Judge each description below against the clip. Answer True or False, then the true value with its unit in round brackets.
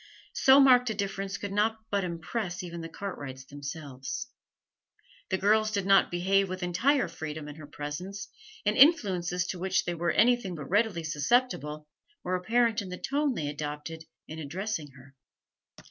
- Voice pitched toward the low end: False (185 Hz)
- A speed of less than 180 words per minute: True (160 wpm)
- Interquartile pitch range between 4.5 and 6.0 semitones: True (5.2 semitones)